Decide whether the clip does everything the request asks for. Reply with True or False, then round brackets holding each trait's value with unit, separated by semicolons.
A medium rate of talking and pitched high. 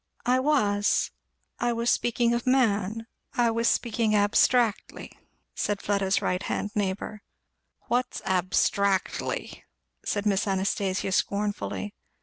False (110 wpm; 210 Hz)